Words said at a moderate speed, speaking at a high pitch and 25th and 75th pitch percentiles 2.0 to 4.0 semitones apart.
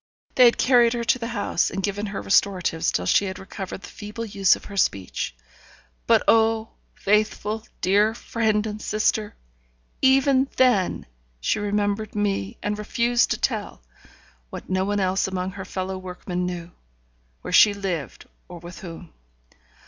Yes: average, 155 wpm; high, 205 Hz; average, 2.9 semitones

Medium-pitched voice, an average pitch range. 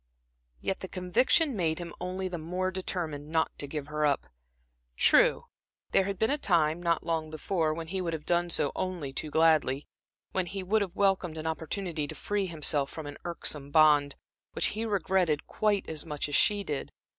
Yes: medium, 170 Hz; average, 3.5 semitones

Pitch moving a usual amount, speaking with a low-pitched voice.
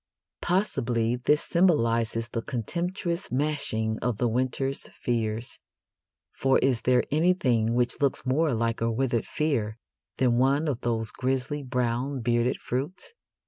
Yes: average, 3.6 semitones; low, 125 Hz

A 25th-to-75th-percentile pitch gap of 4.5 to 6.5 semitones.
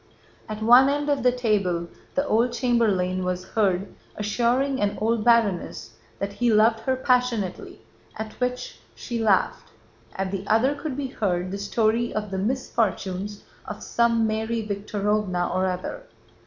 No: average, 3.6 semitones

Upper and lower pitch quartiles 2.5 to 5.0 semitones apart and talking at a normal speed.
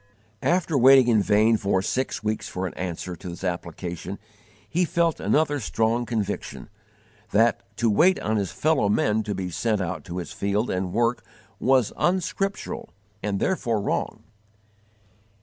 No: wide, 5.6 semitones; average, 150 wpm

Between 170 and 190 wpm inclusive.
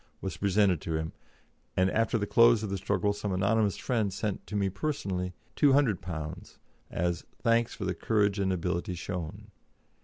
No: average, 160 wpm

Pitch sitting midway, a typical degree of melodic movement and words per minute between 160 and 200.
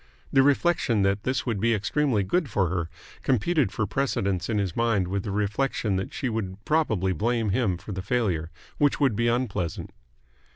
No: low, 110 Hz; average, 5.0 semitones; average, 180 wpm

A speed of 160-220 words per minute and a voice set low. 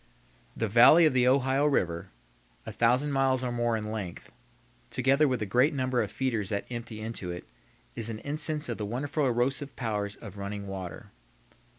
Yes: average, 180 wpm; low, 120 Hz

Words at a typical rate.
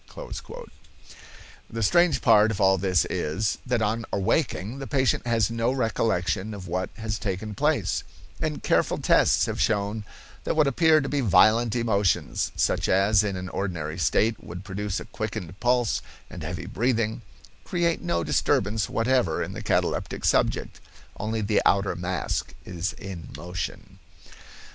Yes: average, 150 wpm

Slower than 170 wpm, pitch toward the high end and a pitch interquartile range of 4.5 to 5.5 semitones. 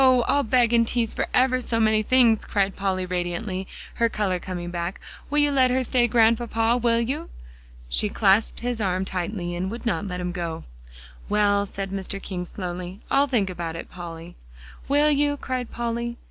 No: average, 180 wpm; high, 215 Hz; average, 4.8 semitones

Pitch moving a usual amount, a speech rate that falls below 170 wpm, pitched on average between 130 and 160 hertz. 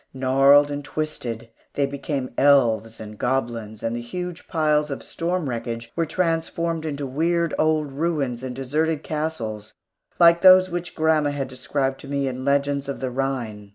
Yes: average, 3.9 semitones; average, 160 wpm; medium, 140 Hz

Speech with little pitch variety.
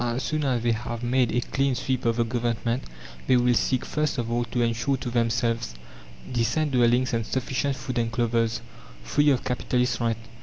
Yes: narrow, 1.7 semitones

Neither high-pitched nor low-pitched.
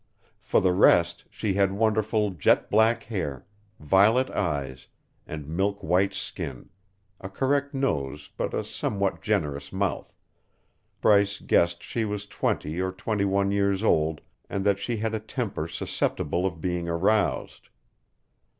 No: low, 100 Hz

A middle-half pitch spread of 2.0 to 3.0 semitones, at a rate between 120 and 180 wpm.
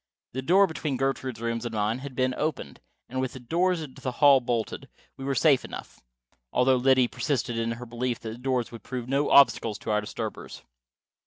No: narrow, 2.5 semitones; average, 195 wpm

